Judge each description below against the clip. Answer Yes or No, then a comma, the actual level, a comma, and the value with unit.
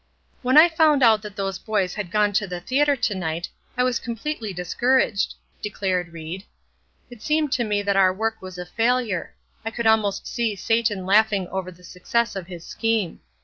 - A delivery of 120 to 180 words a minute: No, average, 190 wpm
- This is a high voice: Yes, high, 210 Hz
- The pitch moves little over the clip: No, average, 4.0 semitones